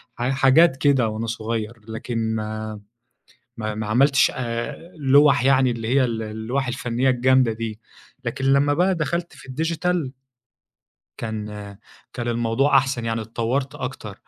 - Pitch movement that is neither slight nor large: Yes, average, 3.4 semitones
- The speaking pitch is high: No, low, 120 Hz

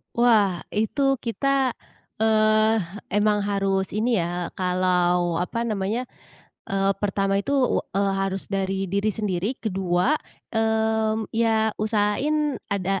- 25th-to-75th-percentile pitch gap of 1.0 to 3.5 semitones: Yes, narrow, 2.5 semitones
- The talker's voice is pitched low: No, high, 210 Hz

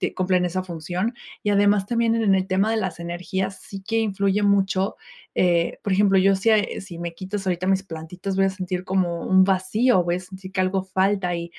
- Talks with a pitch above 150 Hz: Yes, high, 190 Hz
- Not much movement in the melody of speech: Yes, narrow, 1.6 semitones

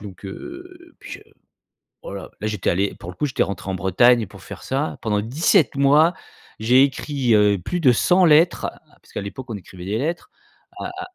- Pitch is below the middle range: Yes, low, 125 Hz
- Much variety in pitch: Yes, wide, 7.6 semitones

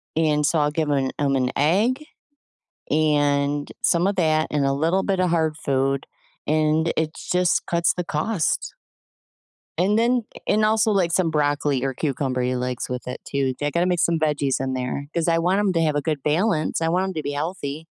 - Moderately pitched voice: Yes, medium, 155 Hz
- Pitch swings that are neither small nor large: Yes, average, 3.6 semitones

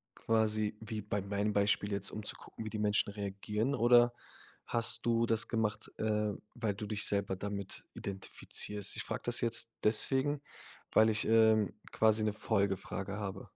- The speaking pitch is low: Yes, low, 105 Hz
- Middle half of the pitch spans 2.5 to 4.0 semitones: No, narrow, 1.7 semitones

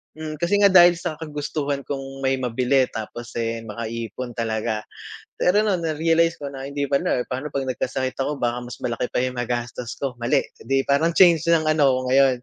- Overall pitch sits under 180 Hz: Yes, low, 135 Hz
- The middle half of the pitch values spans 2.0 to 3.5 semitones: No, average, 4.2 semitones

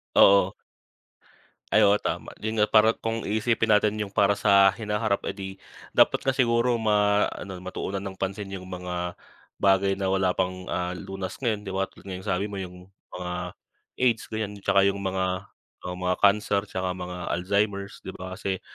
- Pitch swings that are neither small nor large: No, narrow, 2.1 semitones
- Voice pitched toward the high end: No, low, 100 Hz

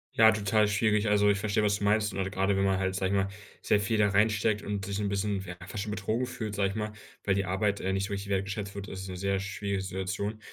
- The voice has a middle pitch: No, low, 100 Hz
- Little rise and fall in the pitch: Yes, narrow, 1.5 semitones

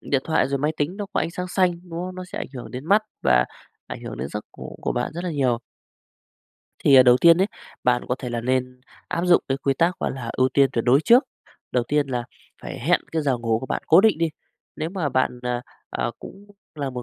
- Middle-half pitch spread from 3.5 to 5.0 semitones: No, wide, 5.5 semitones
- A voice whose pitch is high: No, medium, 140 Hz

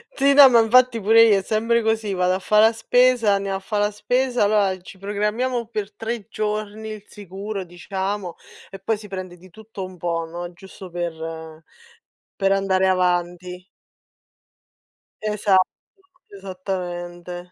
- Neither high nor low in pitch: No, high, 195 Hz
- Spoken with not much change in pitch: No, average, 3.2 semitones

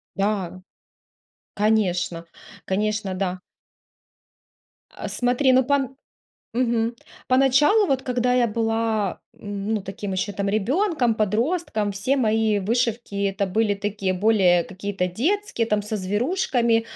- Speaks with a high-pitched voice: Yes, high, 220 Hz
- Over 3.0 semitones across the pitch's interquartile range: Yes, average, 3.9 semitones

